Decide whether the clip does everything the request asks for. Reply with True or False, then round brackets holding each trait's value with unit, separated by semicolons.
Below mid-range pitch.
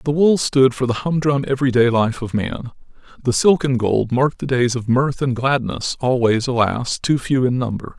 True (125 Hz)